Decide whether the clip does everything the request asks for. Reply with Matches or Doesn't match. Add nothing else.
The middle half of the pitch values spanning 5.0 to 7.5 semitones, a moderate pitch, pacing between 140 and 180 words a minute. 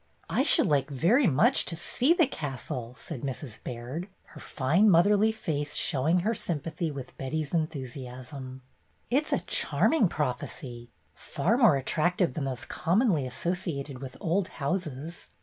Matches